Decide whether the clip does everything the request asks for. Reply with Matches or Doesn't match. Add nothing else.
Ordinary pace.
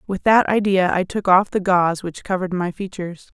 Doesn't match